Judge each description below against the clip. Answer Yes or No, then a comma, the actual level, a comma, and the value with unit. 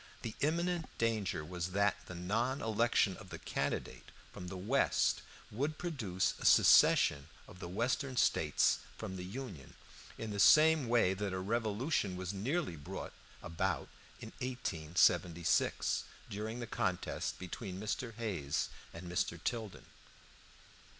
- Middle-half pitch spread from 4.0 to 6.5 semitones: Yes, average, 5.0 semitones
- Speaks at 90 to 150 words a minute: Yes, slow, 135 wpm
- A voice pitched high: No, low, 105 Hz